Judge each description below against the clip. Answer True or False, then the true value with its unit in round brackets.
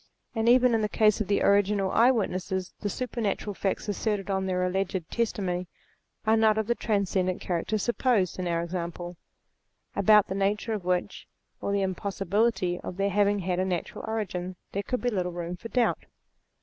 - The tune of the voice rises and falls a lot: False (3.0 semitones)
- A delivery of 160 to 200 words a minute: True (190 wpm)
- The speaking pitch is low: False (200 Hz)